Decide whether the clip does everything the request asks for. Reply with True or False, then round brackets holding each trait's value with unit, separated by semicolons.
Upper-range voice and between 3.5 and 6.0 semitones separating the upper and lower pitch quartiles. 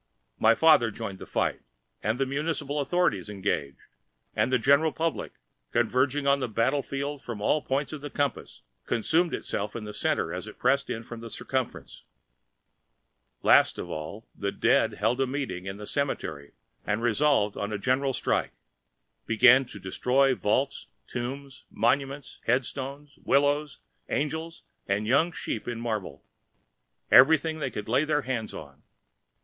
False (130 Hz; 4.3 semitones)